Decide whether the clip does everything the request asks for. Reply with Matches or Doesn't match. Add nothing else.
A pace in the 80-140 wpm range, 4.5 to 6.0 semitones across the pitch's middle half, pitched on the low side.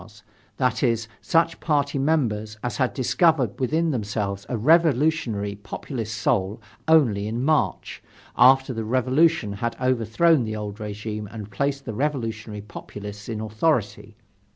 Matches